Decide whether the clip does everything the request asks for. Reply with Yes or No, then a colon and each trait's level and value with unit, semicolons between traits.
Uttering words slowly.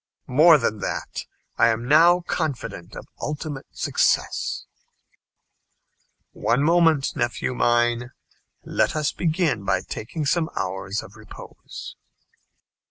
Yes: slow, 105 wpm